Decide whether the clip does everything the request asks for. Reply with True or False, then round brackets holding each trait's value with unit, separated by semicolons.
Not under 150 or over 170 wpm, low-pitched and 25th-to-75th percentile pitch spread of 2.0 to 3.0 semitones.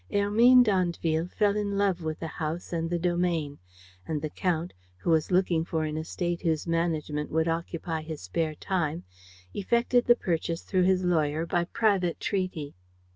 False (165 wpm; 170 Hz; 2.7 semitones)